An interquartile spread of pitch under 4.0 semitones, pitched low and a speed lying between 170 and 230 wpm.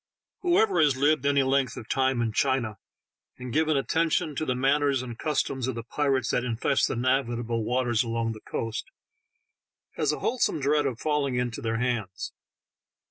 Yes: average, 3.3 semitones; low, 130 Hz; average, 175 wpm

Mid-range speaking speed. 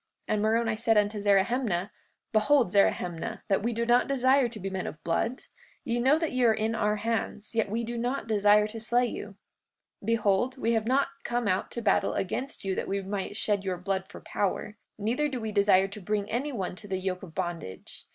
No: fast, 215 wpm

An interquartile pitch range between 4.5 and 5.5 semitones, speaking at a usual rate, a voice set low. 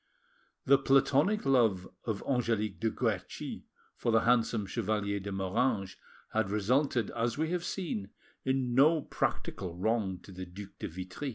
Yes: average, 5.2 semitones; average, 150 wpm; low, 115 Hz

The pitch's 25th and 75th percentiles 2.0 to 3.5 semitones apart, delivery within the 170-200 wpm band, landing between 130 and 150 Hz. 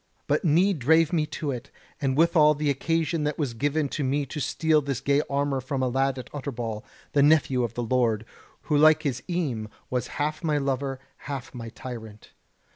Yes: average, 3.1 semitones; average, 195 wpm; medium, 140 Hz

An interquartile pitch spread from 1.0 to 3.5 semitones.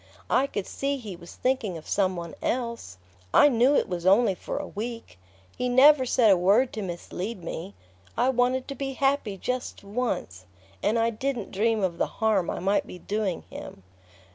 No: wide, 5.6 semitones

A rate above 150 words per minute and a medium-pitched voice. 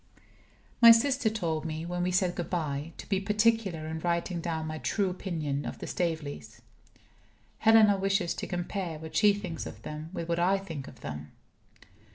Yes: average, 180 wpm; medium, 175 Hz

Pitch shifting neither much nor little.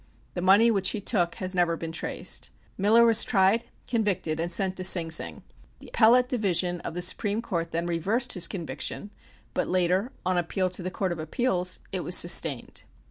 Yes: average, 3.4 semitones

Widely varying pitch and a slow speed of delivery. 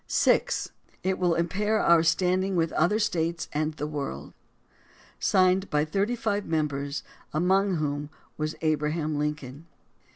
No: average, 3.8 semitones; slow, 130 wpm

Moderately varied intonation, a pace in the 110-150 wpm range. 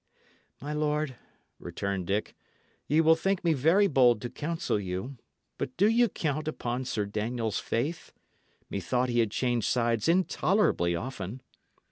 No: wide, 6.0 semitones; average, 140 wpm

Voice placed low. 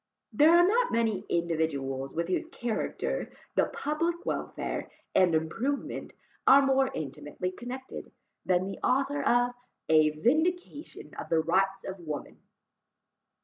No: high, 195 Hz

